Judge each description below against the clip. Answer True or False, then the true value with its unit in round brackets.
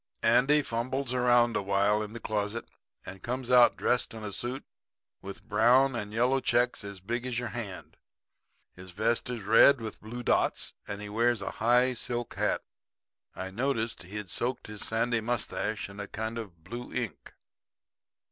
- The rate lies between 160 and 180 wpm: True (165 wpm)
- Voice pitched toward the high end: False (115 Hz)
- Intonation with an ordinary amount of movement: True (3.0 semitones)